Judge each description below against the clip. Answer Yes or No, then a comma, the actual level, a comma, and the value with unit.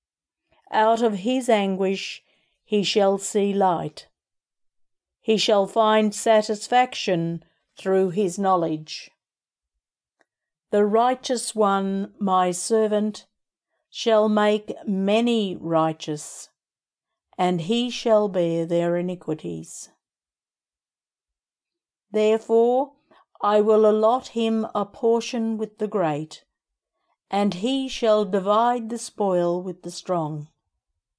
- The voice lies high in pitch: Yes, high, 205 Hz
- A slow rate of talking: Yes, slow, 95 wpm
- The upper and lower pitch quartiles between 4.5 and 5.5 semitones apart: No, average, 3.9 semitones